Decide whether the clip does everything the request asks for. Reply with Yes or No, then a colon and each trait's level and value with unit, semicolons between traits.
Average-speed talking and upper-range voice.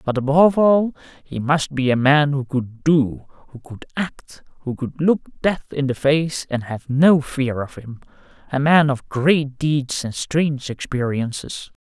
No: average, 180 wpm; medium, 140 Hz